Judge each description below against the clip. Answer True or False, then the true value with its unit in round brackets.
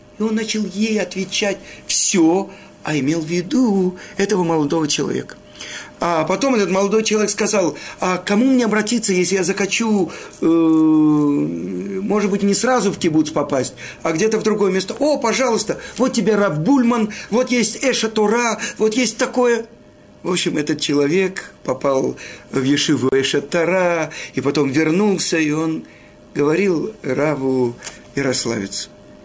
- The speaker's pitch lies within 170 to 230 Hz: True (190 Hz)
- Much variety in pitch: True (5.7 semitones)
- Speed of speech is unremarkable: True (135 wpm)